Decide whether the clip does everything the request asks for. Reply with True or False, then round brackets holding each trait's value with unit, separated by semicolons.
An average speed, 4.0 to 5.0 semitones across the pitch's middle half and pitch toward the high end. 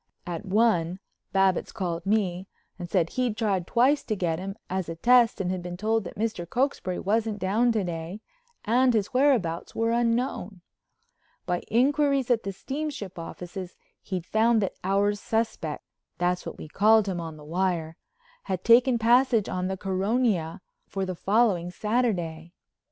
True (150 wpm; 4.6 semitones; 200 Hz)